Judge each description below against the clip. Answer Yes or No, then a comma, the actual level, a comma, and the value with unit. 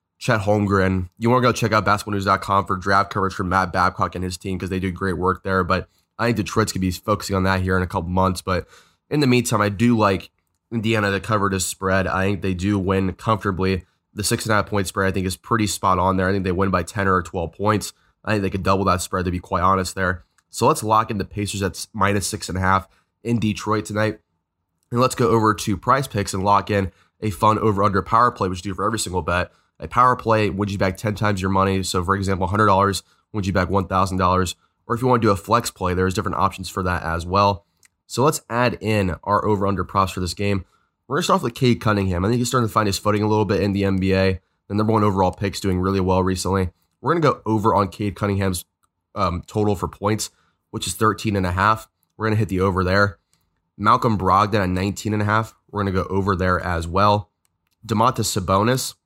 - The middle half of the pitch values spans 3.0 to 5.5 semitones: No, narrow, 2.4 semitones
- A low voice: Yes, low, 100 Hz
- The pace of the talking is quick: Yes, fast, 245 wpm